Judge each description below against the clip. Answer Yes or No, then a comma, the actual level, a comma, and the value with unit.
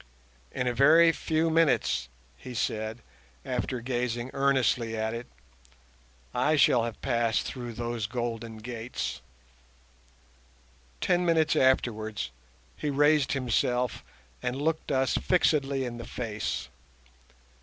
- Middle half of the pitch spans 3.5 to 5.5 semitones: No, average, 3.1 semitones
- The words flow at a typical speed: No, slow, 110 wpm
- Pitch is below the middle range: Yes, low, 125 Hz